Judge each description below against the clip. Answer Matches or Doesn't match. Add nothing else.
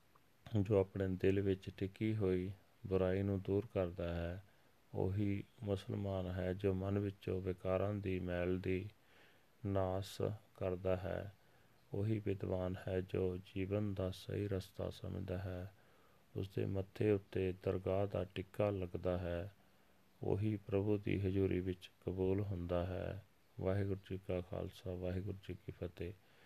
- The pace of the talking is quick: Doesn't match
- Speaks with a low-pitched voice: Matches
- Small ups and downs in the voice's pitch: Matches